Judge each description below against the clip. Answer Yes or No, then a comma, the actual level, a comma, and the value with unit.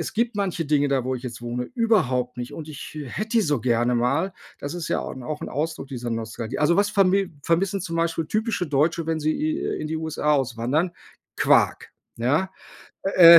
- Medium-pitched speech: Yes, medium, 155 Hz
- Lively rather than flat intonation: Yes, wide, 6.4 semitones